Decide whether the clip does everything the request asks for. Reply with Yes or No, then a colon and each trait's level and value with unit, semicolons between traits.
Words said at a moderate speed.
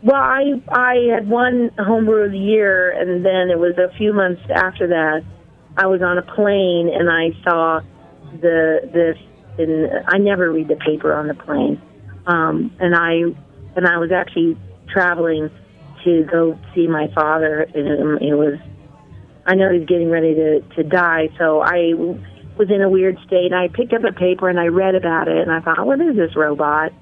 Yes: average, 195 wpm